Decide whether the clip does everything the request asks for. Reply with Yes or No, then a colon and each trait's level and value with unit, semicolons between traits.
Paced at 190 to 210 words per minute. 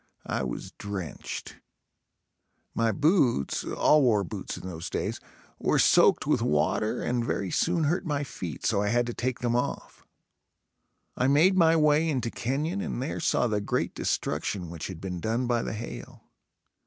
No: average, 165 wpm